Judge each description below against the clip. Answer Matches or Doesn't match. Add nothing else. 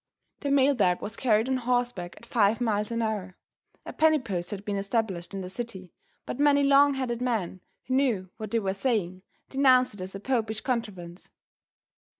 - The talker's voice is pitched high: Matches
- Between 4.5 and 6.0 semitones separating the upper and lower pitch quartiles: Matches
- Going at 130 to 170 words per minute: Doesn't match